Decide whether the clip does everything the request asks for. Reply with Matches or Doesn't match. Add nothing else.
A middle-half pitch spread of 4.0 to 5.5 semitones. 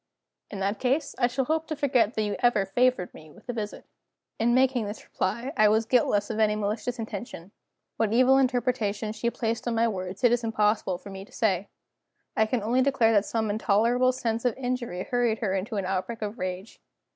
Doesn't match